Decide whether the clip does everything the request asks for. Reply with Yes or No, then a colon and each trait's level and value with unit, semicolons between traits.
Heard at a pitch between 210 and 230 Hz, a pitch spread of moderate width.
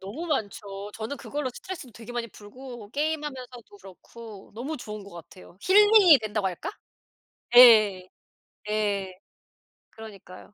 Yes: high, 220 Hz; average, 4.9 semitones